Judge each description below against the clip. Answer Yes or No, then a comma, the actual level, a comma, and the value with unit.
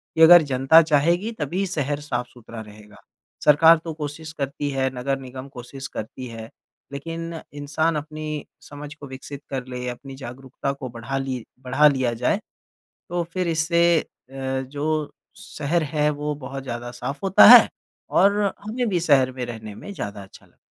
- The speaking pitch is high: No, medium, 140 Hz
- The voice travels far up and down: No, average, 3.8 semitones